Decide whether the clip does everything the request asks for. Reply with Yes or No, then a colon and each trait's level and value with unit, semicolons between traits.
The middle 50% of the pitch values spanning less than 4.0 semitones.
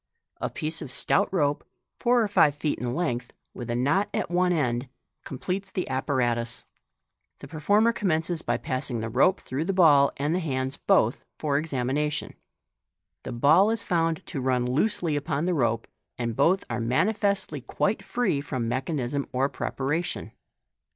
No: wide, 5.6 semitones